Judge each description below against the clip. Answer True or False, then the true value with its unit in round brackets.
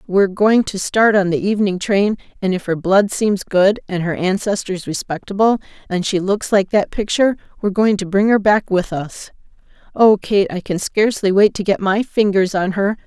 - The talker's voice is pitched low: False (195 Hz)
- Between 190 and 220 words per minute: True (200 wpm)